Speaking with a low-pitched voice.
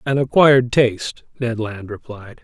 Yes: low, 120 Hz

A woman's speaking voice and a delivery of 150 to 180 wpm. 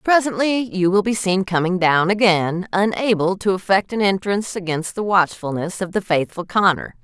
Yes: female; average, 170 wpm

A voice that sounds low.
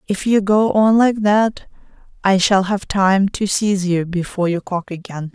No: high, 195 Hz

